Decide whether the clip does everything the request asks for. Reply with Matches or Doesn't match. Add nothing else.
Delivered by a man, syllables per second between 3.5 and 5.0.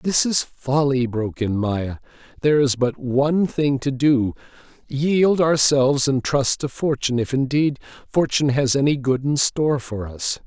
Matches